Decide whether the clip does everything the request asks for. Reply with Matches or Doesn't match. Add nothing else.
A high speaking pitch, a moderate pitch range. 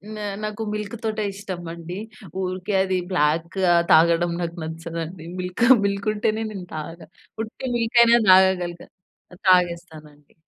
Doesn't match